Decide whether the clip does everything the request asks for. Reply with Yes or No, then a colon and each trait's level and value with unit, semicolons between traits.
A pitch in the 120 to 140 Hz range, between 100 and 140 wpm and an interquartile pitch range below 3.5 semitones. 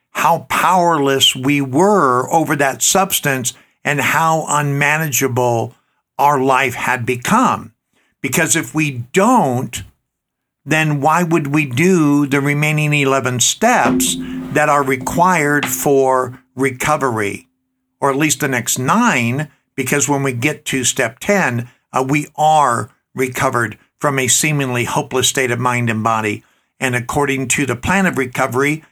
Yes: low, 135 Hz; slow, 135 wpm; average, 3.1 semitones